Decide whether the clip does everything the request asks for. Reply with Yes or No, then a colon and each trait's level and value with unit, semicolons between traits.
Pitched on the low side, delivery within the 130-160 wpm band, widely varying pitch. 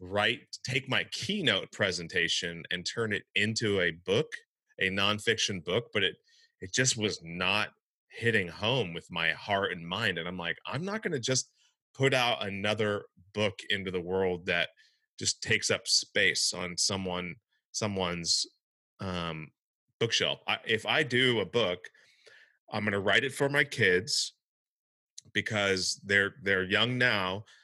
Yes: low, 105 Hz; average, 150 wpm; wide, 5.7 semitones